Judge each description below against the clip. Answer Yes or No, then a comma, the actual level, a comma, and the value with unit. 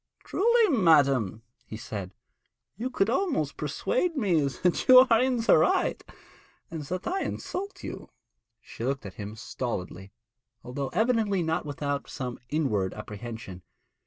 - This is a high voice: No, medium, 150 Hz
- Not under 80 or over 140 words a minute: Yes, slow, 135 wpm